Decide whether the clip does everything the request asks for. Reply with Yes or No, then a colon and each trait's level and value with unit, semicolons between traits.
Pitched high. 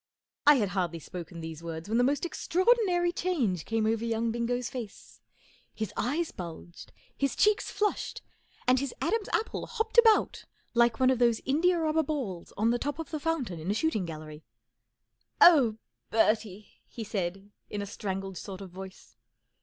Yes: high, 230 Hz